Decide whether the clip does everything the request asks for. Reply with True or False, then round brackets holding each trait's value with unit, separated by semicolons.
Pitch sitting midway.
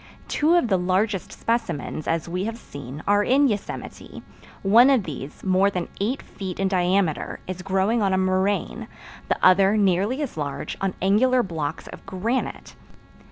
False (195 Hz)